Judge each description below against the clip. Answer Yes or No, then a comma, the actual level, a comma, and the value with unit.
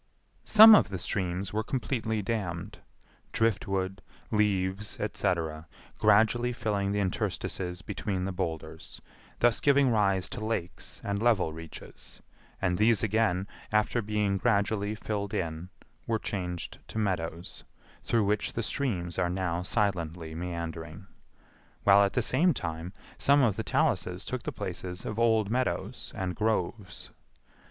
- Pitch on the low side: Yes, low, 100 Hz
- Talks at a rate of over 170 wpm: No, slow, 135 wpm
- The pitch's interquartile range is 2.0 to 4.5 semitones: Yes, average, 3.7 semitones